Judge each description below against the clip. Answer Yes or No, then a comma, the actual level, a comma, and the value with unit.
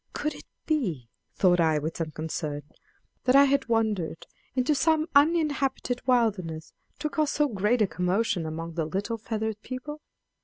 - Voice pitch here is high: Yes, high, 220 Hz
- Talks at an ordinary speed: Yes, average, 155 wpm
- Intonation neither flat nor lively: No, wide, 8.8 semitones